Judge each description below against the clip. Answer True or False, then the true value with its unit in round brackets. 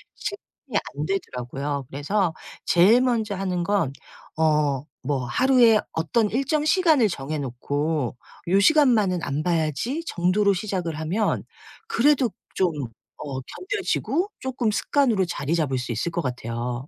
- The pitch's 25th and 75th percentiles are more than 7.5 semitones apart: True (8.3 semitones)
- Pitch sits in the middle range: True (180 Hz)